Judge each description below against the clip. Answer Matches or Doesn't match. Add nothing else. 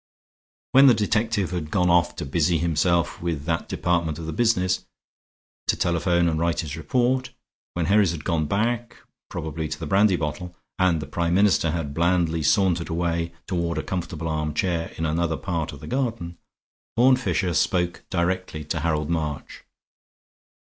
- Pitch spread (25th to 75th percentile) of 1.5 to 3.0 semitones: Matches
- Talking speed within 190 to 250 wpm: Doesn't match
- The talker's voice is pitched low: Matches